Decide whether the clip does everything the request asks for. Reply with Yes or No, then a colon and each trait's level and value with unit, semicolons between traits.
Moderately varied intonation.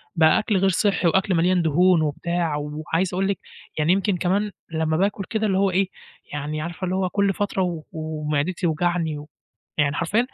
Yes: average, 3.4 semitones